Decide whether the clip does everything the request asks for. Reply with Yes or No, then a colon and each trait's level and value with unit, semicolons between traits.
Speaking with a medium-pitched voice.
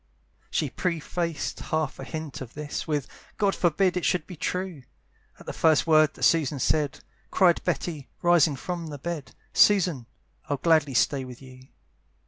Yes: medium, 155 Hz